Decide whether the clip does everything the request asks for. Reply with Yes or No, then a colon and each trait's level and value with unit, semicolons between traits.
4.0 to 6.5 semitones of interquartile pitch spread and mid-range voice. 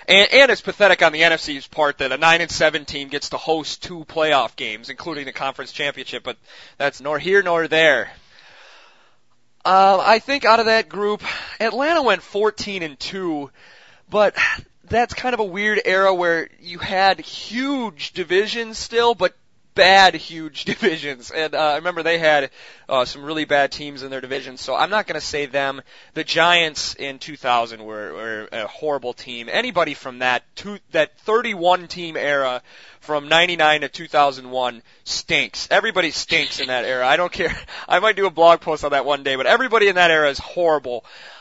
Yes: wide, 5.6 semitones; medium, 160 Hz